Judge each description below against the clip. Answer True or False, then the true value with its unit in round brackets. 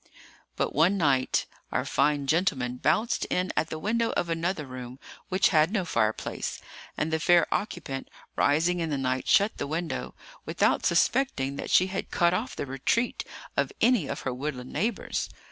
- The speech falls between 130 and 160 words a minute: False (170 wpm)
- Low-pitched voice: False (160 Hz)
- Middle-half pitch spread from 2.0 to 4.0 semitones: False (5.5 semitones)